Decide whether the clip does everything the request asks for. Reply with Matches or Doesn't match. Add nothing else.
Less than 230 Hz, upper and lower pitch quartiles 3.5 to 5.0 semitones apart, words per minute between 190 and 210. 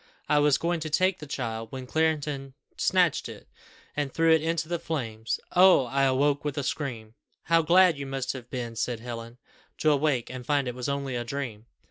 Matches